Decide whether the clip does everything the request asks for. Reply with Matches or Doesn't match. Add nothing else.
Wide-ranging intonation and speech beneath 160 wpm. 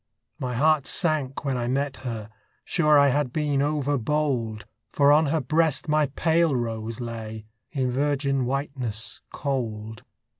Doesn't match